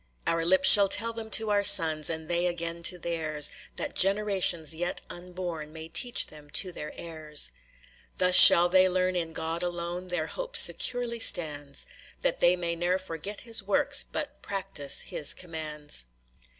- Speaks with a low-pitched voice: No, medium, 175 Hz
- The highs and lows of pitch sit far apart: No, average, 3.3 semitones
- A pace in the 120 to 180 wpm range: Yes, average, 165 wpm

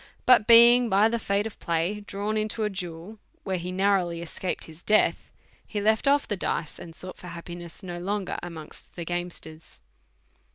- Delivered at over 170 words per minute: Yes, average, 180 wpm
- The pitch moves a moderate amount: Yes, average, 3.7 semitones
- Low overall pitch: No, high, 190 Hz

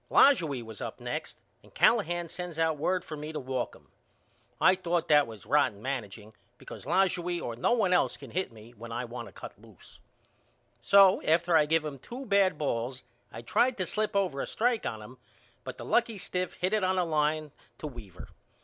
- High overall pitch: No, medium, 155 Hz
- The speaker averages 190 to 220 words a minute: Yes, fast, 205 wpm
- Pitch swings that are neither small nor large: No, wide, 6.8 semitones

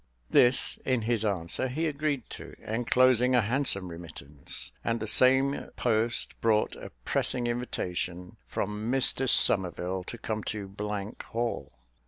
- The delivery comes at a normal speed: No, slow, 130 wpm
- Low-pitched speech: Yes, low, 115 Hz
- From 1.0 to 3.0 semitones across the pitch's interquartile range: No, average, 4.3 semitones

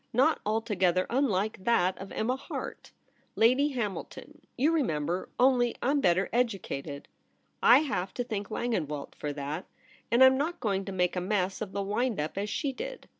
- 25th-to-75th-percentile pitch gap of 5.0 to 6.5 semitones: Yes, wide, 5.6 semitones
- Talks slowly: No, average, 180 wpm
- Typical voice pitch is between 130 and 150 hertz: No, high, 215 Hz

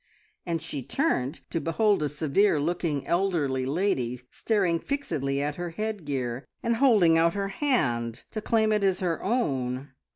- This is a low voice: No, medium, 165 Hz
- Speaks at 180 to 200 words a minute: No, average, 155 wpm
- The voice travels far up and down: Yes, wide, 6.7 semitones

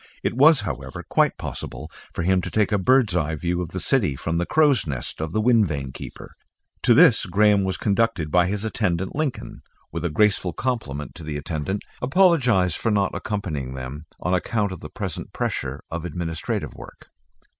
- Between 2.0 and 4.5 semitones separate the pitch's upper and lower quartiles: No, wide, 5.6 semitones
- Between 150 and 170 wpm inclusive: No, average, 190 wpm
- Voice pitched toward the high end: No, very low, 90 Hz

